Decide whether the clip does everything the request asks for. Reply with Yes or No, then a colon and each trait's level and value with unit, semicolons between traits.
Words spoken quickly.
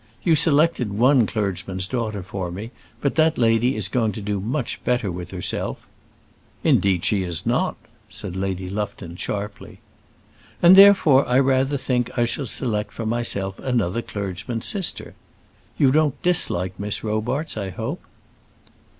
No: average, 150 wpm